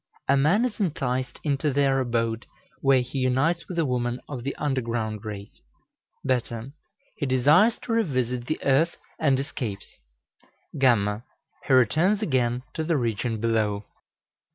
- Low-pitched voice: Yes, low, 130 Hz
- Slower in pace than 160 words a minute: Yes, average, 140 wpm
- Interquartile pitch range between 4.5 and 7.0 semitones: No, average, 3.8 semitones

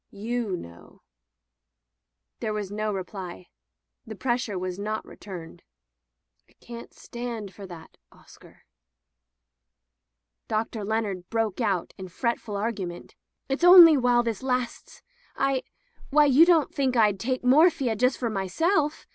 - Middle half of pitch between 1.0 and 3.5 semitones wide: No, average, 4.7 semitones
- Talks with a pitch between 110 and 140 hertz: No, high, 225 Hz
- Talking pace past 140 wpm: No, slow, 135 wpm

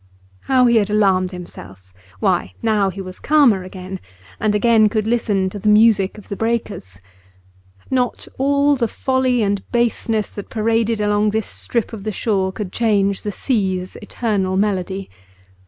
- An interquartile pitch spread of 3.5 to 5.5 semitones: No, average, 3.1 semitones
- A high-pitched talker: Yes, high, 210 Hz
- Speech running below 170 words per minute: Yes, average, 155 wpm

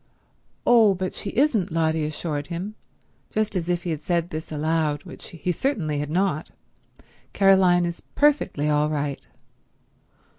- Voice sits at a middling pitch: Yes, medium, 170 Hz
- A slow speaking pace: No, average, 145 wpm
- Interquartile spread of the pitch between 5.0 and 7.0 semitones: No, average, 4.0 semitones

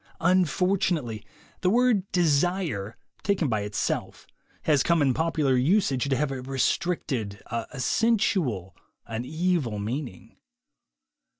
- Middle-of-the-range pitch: Yes, medium, 145 Hz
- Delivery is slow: Yes, slow, 115 wpm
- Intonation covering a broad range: Yes, wide, 7.1 semitones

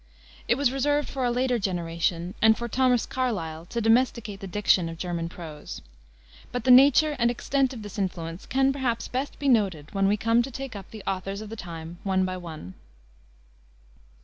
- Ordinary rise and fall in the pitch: No, wide, 6.1 semitones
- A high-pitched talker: Yes, high, 215 Hz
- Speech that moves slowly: No, average, 190 wpm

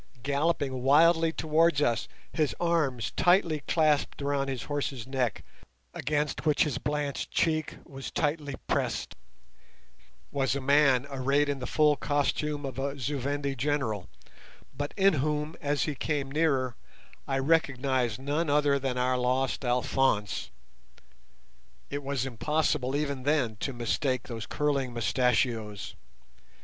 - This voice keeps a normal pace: No, slow, 130 wpm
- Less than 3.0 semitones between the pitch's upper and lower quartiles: Yes, narrow, 2.5 semitones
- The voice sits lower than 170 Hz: Yes, medium, 140 Hz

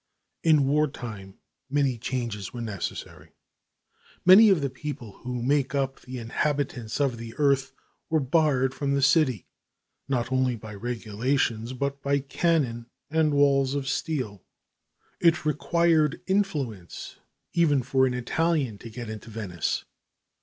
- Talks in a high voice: No, low, 135 Hz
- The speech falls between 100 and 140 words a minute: Yes, slow, 135 wpm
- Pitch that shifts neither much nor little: Yes, average, 3.8 semitones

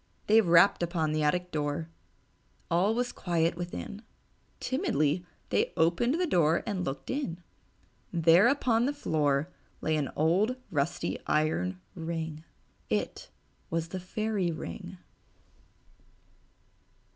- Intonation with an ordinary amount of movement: Yes, average, 4.6 semitones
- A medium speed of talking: No, slow, 115 wpm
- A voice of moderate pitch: Yes, medium, 170 Hz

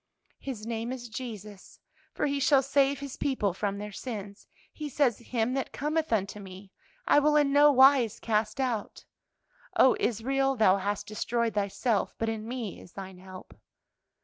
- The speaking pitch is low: No, high, 230 Hz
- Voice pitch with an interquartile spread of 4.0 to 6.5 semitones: Yes, average, 4.7 semitones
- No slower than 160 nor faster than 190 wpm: Yes, average, 165 wpm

